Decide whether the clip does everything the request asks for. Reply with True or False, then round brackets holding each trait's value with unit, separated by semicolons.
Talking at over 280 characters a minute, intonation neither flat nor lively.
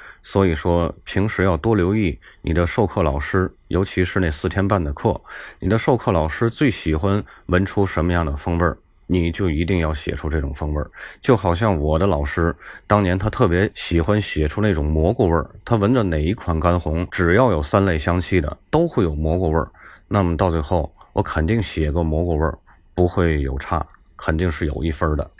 True (295 characters per minute; 3.6 semitones)